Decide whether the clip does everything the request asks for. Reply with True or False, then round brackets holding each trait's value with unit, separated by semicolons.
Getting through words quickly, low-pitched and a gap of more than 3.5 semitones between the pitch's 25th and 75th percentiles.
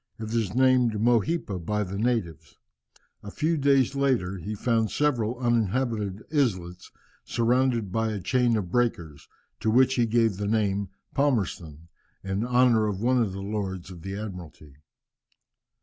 False (150 wpm; 110 Hz; 4.1 semitones)